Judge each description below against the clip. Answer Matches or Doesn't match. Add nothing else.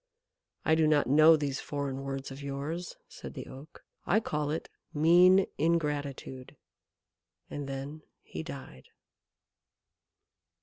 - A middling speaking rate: Doesn't match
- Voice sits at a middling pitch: Matches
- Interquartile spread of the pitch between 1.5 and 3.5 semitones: Matches